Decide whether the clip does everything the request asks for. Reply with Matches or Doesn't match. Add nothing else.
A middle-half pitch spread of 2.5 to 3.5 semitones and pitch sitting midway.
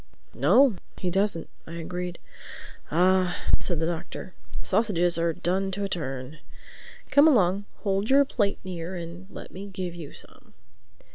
Matches